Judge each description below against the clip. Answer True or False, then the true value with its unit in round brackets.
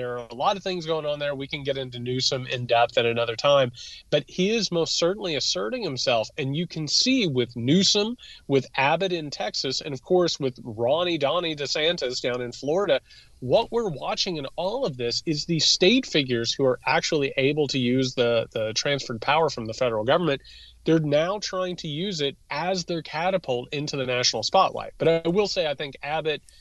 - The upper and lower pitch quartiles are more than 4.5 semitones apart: True (5.2 semitones)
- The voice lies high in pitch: False (145 Hz)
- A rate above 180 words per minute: True (205 wpm)